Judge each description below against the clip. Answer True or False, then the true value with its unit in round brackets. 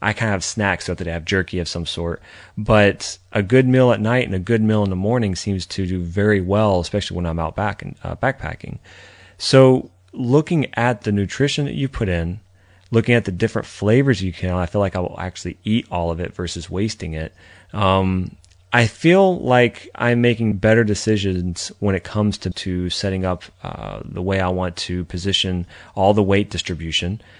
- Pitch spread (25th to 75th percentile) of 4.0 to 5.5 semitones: False (3.6 semitones)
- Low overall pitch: True (95 Hz)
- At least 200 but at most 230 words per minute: True (205 wpm)